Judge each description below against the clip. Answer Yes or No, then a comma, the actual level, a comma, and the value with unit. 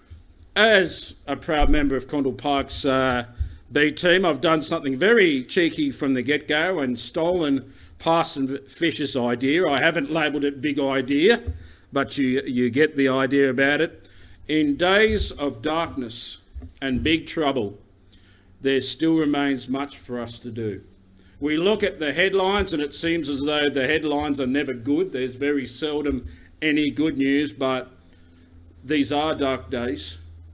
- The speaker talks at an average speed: Yes, average, 155 wpm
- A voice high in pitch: No, medium, 140 Hz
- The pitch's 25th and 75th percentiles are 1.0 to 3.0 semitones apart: No, average, 4.0 semitones